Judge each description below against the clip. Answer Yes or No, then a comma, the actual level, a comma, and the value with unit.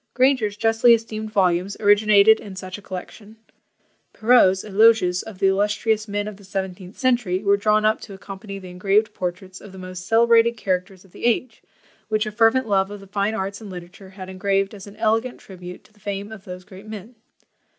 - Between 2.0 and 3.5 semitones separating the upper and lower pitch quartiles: Yes, narrow, 2.5 semitones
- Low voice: No, high, 205 Hz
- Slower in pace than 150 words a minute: No, average, 200 wpm